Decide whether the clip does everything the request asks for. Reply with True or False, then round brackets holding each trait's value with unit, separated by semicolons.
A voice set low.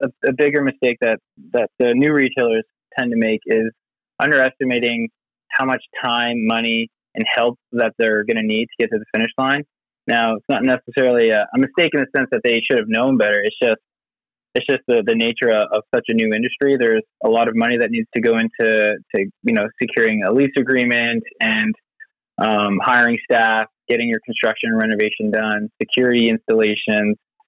True (115 Hz)